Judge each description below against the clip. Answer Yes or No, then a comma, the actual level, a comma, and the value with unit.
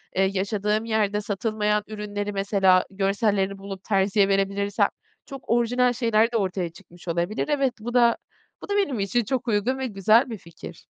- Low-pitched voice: No, high, 210 Hz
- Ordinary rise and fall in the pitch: Yes, average, 3.0 semitones